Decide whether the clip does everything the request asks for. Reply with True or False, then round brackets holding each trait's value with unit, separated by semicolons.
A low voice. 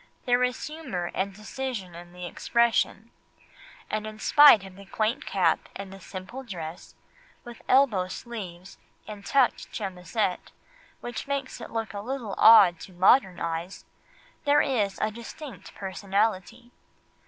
False (210 Hz)